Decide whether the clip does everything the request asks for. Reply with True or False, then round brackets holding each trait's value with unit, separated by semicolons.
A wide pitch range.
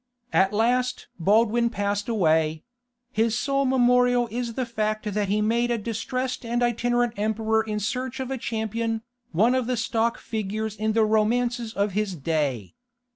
False (2.4 semitones)